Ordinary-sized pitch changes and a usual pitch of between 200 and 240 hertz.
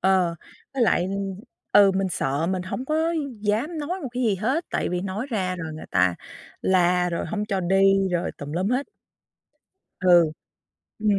No: average, 3.8 semitones; high, 190 Hz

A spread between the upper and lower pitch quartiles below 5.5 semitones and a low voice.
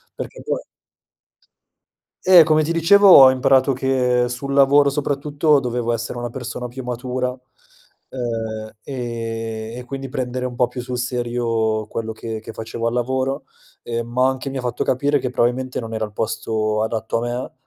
Yes: narrow, 2.5 semitones; low, 125 Hz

